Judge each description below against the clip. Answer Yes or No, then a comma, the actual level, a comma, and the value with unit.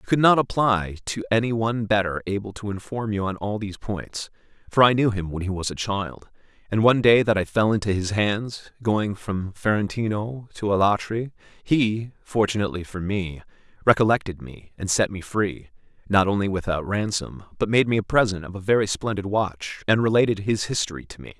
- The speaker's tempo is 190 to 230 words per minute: Yes, average, 195 wpm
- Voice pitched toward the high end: No, low, 105 Hz